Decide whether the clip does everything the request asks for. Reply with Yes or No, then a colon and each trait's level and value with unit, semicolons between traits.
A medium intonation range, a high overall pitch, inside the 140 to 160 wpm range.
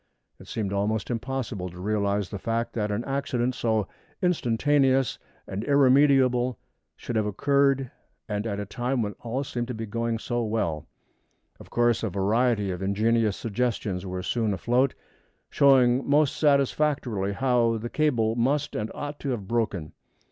No: average, 4.1 semitones; low, 115 Hz; average, 155 wpm